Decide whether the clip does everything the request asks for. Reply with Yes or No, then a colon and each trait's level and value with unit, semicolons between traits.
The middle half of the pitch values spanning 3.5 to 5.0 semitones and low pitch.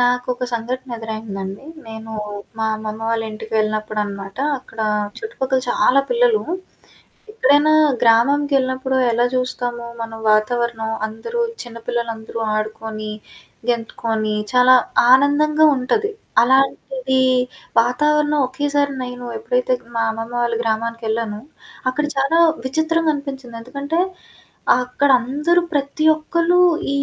No: average, 4.3 semitones; very high, 250 Hz